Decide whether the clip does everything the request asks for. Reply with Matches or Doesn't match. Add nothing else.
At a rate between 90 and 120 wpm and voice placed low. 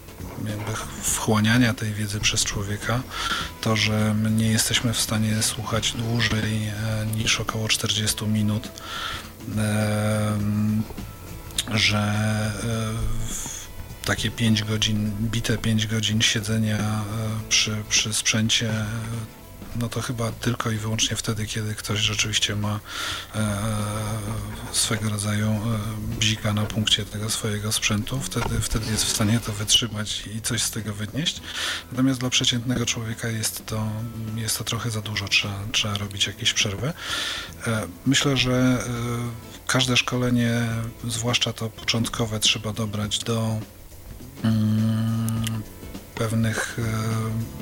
Matches